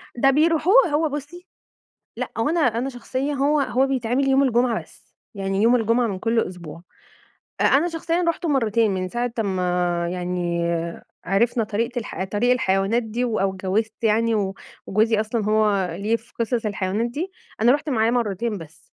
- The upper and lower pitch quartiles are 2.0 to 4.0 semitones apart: No, average, 5.0 semitones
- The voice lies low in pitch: No, high, 230 Hz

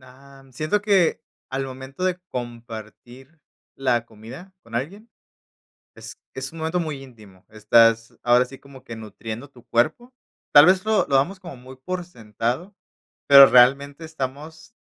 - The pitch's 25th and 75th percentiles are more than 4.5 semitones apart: Yes, average, 5.1 semitones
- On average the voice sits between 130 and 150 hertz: Yes, low, 135 Hz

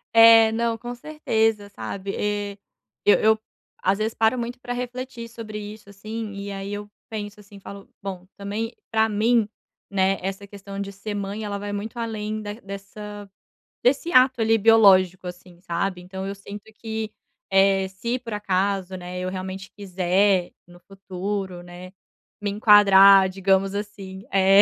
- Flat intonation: Yes, narrow, 2.3 semitones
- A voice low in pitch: No, high, 200 Hz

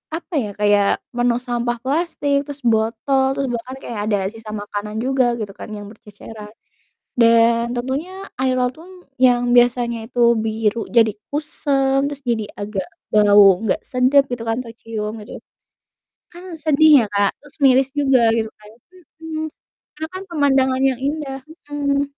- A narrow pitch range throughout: No, average, 4.1 semitones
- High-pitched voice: Yes, high, 245 Hz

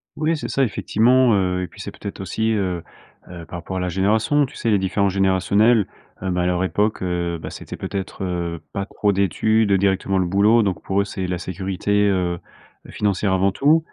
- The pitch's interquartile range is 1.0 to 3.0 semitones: Yes, narrow, 2.6 semitones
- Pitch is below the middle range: Yes, very low, 95 Hz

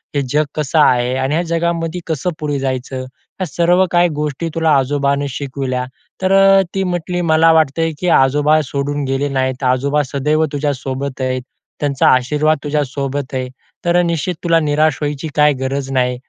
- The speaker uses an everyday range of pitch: Yes, average, 3.4 semitones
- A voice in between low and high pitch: Yes, medium, 145 Hz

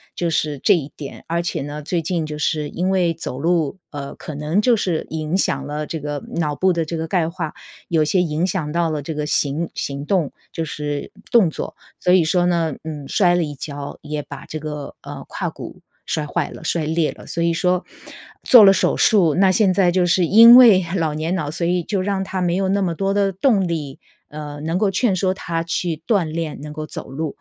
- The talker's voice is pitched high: No, medium, 165 Hz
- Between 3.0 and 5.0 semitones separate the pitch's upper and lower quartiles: Yes, average, 3.4 semitones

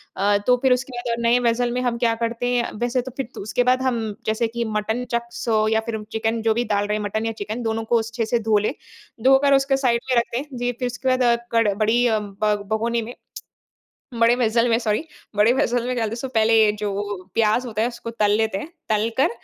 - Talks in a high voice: Yes, high, 230 Hz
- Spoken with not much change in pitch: Yes, narrow, 2.0 semitones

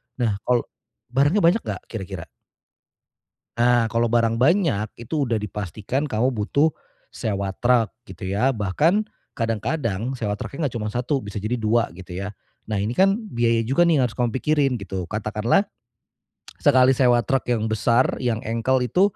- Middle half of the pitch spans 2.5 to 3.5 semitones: No, average, 3.9 semitones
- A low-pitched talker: Yes, low, 120 Hz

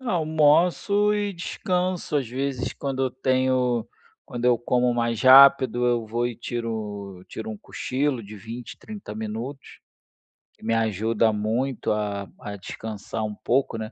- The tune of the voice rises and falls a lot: No, average, 3.8 semitones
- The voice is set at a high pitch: No, low, 120 Hz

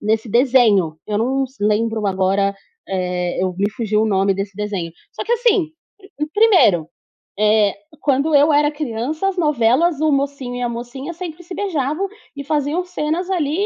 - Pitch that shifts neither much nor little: No, wide, 6.7 semitones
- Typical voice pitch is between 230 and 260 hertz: Yes, very high, 255 Hz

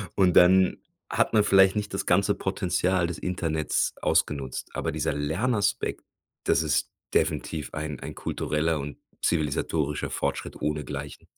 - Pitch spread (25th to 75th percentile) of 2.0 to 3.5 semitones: No, average, 3.9 semitones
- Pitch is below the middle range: Yes, very low, 80 Hz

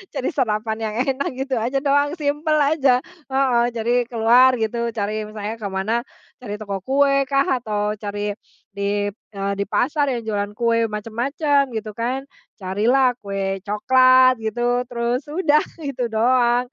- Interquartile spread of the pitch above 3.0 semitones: Yes, average, 3.9 semitones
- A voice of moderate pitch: No, high, 235 Hz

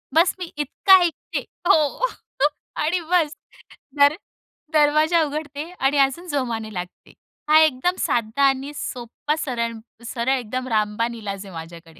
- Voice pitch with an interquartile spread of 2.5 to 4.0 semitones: No, average, 5.0 semitones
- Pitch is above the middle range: Yes, very high, 275 Hz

